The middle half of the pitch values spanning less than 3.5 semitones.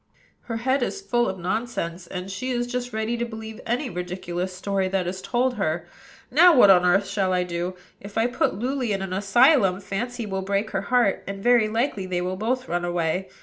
No: average, 4.6 semitones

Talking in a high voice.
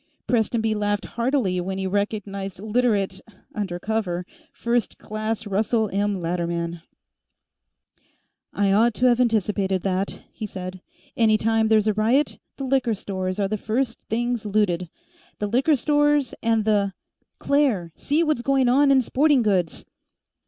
Yes: high, 215 Hz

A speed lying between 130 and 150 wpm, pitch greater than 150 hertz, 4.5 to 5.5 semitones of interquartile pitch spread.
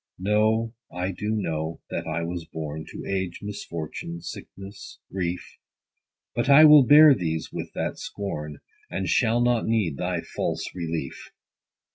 No: average, 145 wpm; very low, 95 Hz; average, 5.0 semitones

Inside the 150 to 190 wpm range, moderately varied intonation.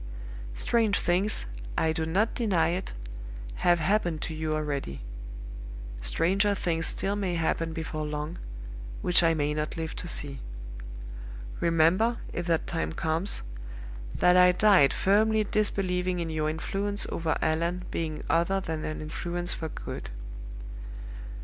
No: slow, 135 wpm; average, 3.2 semitones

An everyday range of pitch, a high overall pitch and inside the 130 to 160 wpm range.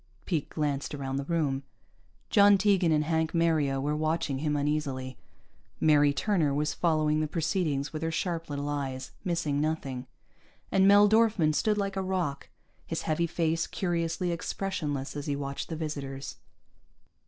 No: average, 3.1 semitones; medium, 155 Hz; average, 155 wpm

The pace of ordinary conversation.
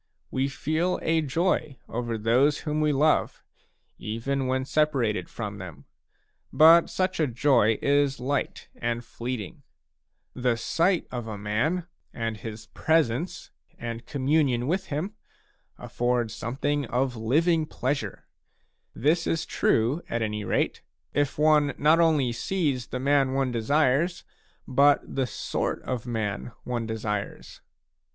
No: slow, 130 wpm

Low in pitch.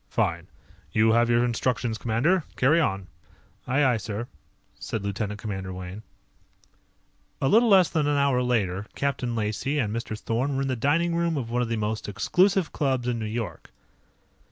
Yes: low, 120 Hz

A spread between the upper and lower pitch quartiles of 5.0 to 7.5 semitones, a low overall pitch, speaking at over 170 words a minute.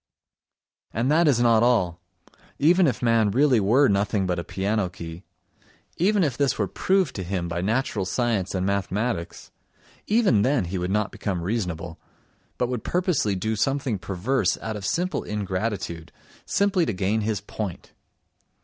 No: wide, 5.6 semitones; low, 110 Hz; average, 160 wpm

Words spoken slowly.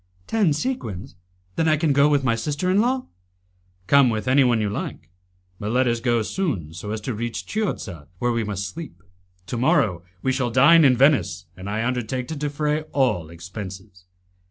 No: average, 180 wpm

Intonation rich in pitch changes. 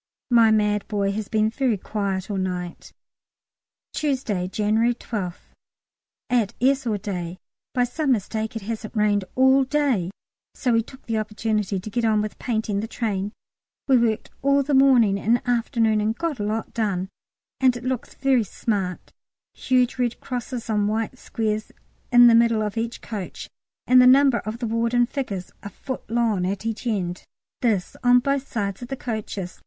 No: average, 3.1 semitones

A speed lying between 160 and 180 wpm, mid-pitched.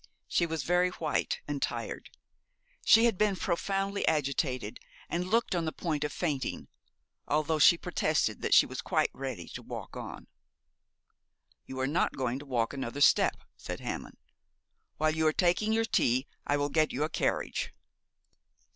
Yes: average, 165 wpm; medium, 155 Hz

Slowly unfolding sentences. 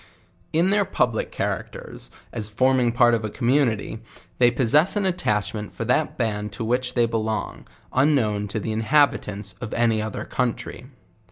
No: average, 160 wpm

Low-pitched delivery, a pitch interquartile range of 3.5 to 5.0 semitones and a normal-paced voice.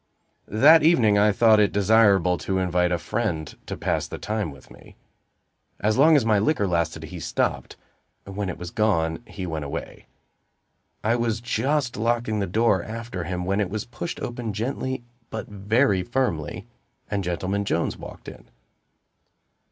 Yes: low, 105 Hz; average, 4.2 semitones; average, 160 wpm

